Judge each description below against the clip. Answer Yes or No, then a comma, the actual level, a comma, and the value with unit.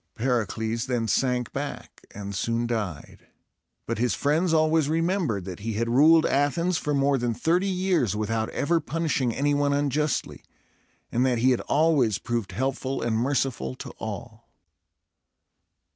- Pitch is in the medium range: No, low, 130 Hz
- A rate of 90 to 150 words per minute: Yes, average, 145 wpm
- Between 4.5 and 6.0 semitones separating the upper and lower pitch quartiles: Yes, average, 5.0 semitones